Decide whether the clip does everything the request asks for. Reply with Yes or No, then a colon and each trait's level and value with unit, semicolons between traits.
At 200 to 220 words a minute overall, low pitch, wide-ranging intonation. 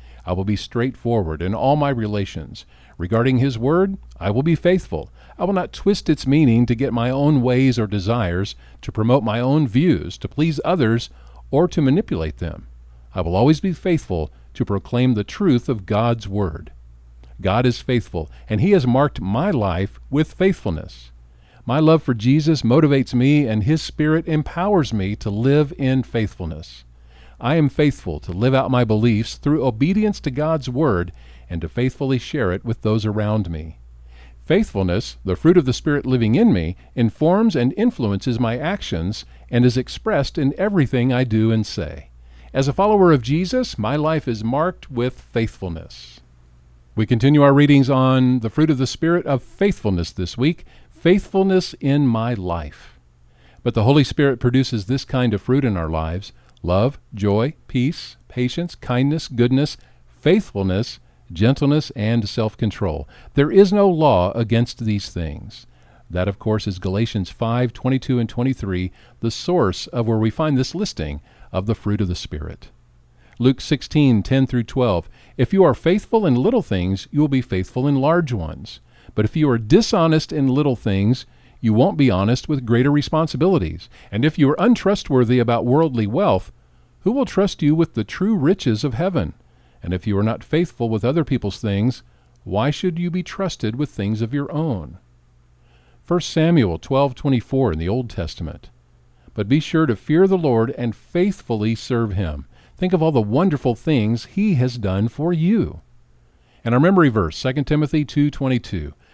No: average, 175 wpm; low, 120 Hz; wide, 7.1 semitones